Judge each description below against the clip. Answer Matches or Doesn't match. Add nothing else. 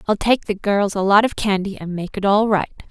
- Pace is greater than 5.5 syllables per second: Doesn't match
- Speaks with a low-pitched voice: Doesn't match